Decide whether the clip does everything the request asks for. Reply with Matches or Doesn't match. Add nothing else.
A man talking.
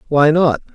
Matches